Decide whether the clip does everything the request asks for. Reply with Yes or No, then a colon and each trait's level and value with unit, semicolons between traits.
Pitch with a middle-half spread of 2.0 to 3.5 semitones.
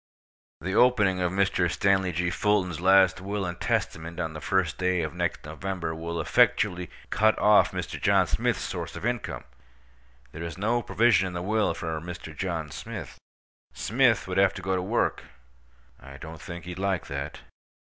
Yes: average, 2.8 semitones